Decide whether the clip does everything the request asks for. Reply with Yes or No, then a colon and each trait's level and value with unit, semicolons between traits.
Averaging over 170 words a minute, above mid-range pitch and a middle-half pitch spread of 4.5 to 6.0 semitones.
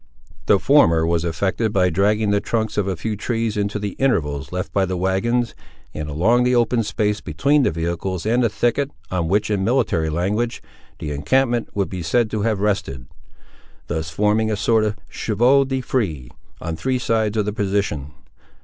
No: average, 185 wpm; low, 105 Hz; average, 4.9 semitones